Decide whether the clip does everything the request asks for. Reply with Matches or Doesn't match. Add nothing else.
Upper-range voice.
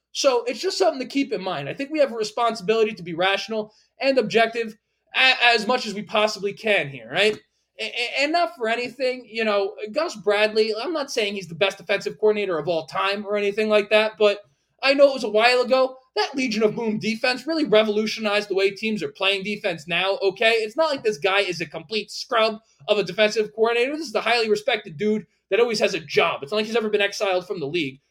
Matches